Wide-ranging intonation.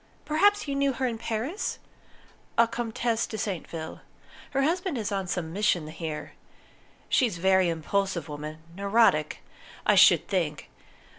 Yes: wide, 6.8 semitones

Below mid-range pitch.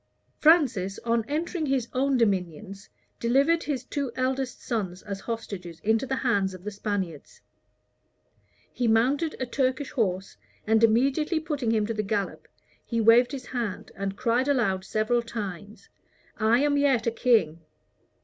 No: high, 230 Hz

